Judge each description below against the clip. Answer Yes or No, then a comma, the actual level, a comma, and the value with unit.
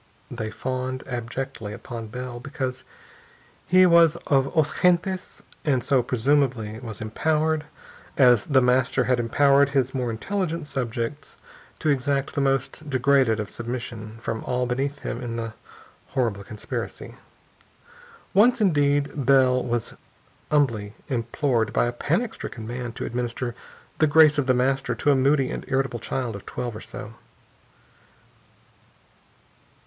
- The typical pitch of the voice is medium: No, low, 130 Hz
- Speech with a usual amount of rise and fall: Yes, average, 3.2 semitones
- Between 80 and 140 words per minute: Yes, slow, 135 wpm